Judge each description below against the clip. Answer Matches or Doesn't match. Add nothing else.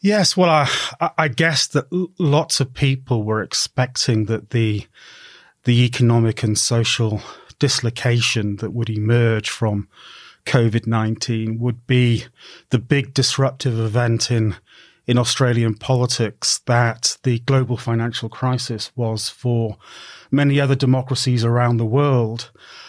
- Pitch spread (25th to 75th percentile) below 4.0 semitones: Matches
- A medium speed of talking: Doesn't match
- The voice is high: Doesn't match